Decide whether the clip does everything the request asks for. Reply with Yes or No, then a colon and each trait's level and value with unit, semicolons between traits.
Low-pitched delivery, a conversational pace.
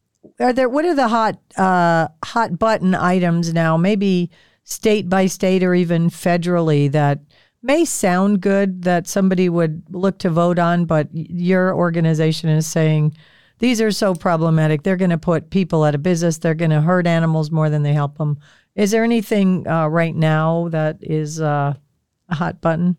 No: medium, 175 Hz; average, 175 wpm